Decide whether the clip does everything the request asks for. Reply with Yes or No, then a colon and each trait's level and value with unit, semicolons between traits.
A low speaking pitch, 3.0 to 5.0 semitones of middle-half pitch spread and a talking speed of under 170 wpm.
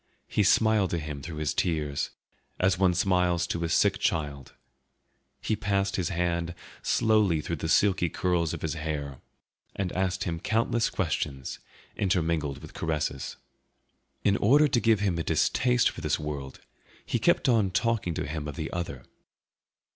Yes: very low, 85 Hz; average, 4.2 semitones; average, 160 wpm